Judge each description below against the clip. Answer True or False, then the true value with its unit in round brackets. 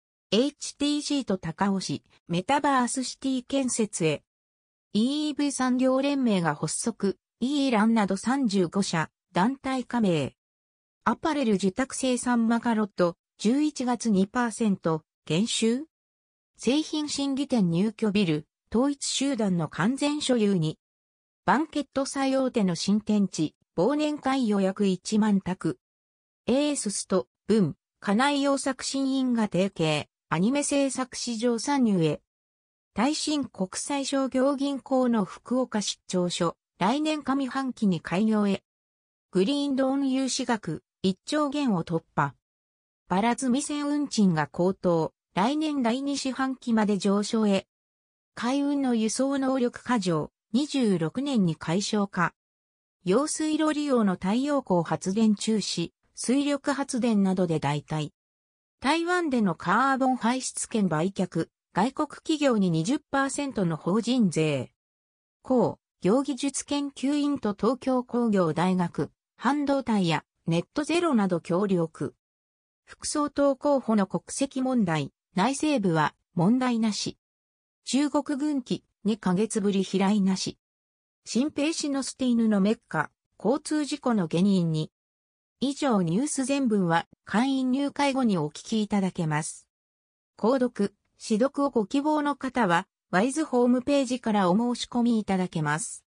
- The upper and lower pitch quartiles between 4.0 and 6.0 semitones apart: False (7.3 semitones)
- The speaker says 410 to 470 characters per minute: False (230 characters per minute)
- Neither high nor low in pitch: False (220 Hz)